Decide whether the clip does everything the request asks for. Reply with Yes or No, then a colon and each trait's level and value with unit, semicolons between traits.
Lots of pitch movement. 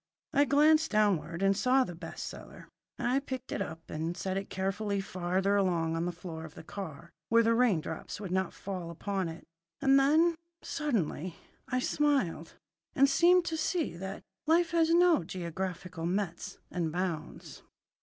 Yes: wide, 7.9 semitones